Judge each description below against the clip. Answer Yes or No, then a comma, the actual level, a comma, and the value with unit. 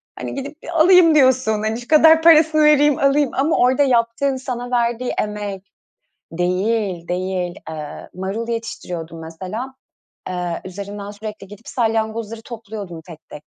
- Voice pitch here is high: Yes, high, 225 Hz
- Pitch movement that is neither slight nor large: No, wide, 5.7 semitones